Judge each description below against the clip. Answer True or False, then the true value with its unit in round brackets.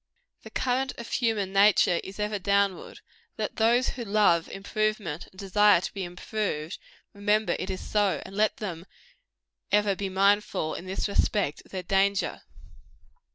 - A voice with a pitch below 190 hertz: False (200 Hz)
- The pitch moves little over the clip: True (2.1 semitones)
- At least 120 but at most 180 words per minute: True (155 wpm)